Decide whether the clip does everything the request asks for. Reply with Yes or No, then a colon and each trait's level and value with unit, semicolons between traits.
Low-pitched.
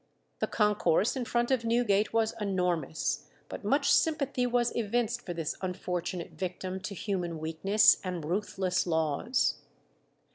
No: high, 195 Hz